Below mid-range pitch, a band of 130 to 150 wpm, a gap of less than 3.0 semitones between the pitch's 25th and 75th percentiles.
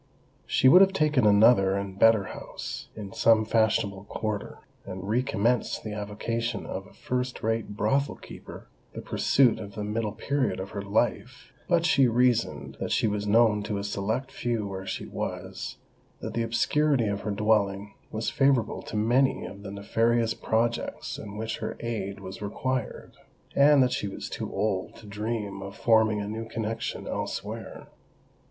No: low, 110 Hz; average, 160 wpm; narrow, 2.6 semitones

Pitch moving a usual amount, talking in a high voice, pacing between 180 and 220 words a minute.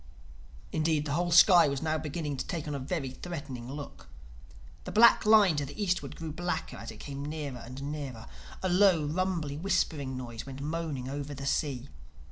No: average, 3.7 semitones; medium, 150 Hz; average, 185 wpm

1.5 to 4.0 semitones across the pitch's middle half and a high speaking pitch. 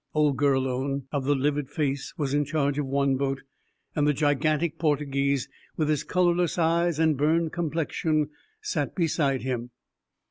No: narrow, 2.4 semitones; medium, 145 Hz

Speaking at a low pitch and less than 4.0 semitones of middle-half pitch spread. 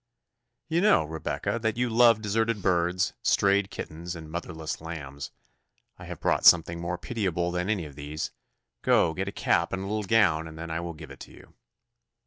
No: very low, 85 Hz; average, 4.4 semitones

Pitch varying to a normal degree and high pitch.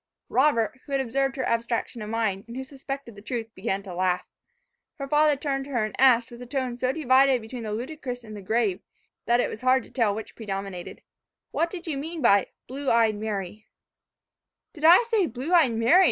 Yes: average, 3.9 semitones; high, 245 Hz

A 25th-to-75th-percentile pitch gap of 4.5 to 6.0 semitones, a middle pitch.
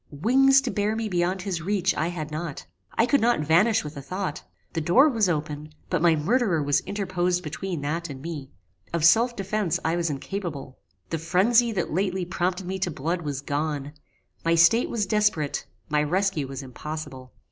Yes: average, 4.8 semitones; medium, 175 Hz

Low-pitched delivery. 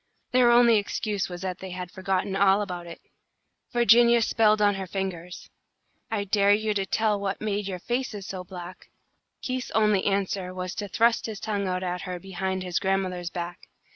No: high, 195 Hz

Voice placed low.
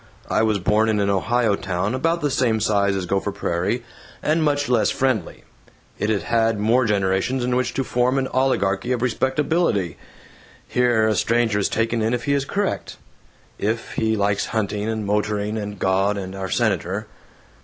Yes: low, 110 Hz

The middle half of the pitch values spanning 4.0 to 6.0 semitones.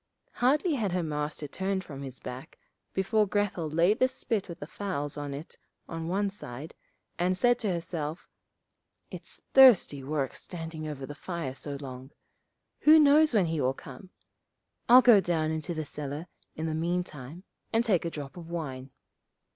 Yes: average, 5.2 semitones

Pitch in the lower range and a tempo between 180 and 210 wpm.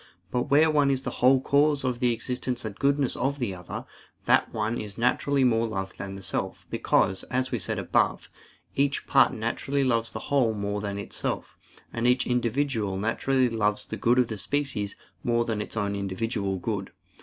Yes: low, 120 Hz; average, 185 wpm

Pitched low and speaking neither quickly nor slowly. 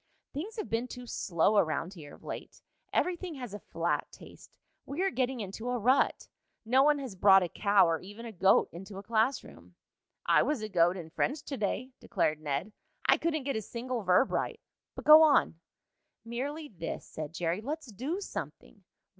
No: high, 230 Hz; average, 190 wpm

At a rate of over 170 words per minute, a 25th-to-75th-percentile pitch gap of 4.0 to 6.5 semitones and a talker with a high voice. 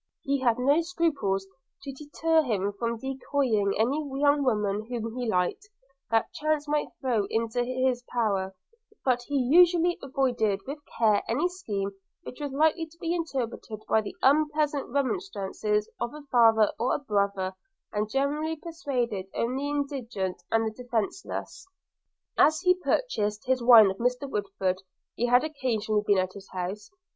No: average, 155 wpm; wide, 5.4 semitones; very high, 250 Hz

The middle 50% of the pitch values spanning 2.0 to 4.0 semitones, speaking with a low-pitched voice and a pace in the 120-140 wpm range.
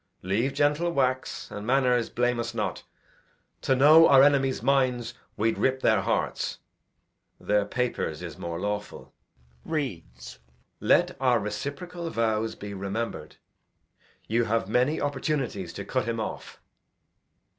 No: average, 4.7 semitones; low, 120 Hz; slow, 135 wpm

